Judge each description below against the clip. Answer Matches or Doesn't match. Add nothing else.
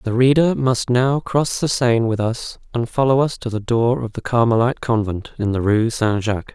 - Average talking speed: Doesn't match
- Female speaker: Doesn't match